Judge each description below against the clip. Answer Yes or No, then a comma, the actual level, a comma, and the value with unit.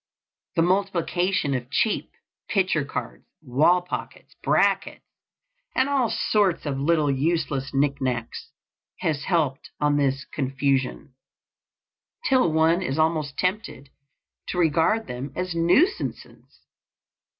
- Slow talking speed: Yes, slow, 105 wpm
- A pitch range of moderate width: Yes, average, 4.8 semitones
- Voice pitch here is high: No, medium, 160 Hz